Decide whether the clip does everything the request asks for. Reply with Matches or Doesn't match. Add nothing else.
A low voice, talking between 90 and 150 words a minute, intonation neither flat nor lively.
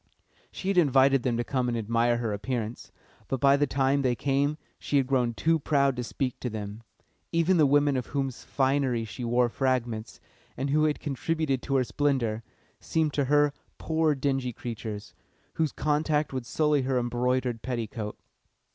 Doesn't match